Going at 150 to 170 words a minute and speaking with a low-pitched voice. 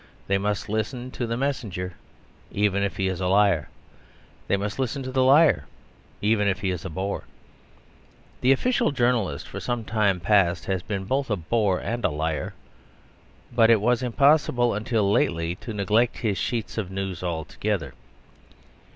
Yes: average, 165 wpm; low, 105 Hz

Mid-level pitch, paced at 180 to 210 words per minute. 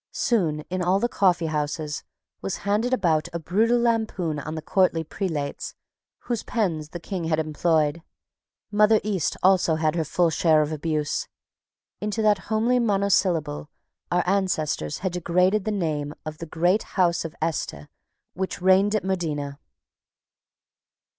No: medium, 175 Hz; average, 140 wpm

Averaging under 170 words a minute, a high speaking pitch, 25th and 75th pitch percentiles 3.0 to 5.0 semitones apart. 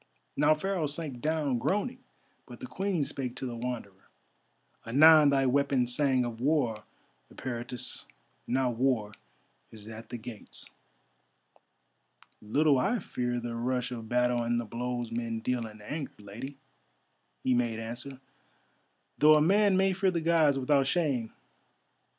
No: average, 140 wpm; low, 125 Hz; average, 4.3 semitones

